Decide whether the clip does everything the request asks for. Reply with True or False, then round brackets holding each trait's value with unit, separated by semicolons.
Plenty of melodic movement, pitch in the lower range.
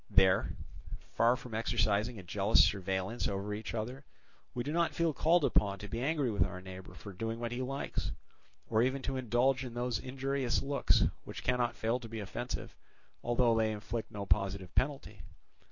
False (3.8 semitones; 115 Hz)